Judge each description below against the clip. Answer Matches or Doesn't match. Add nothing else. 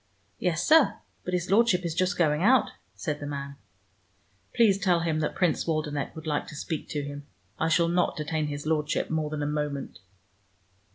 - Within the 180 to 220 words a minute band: Matches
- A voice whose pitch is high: Doesn't match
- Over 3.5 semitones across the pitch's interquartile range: Doesn't match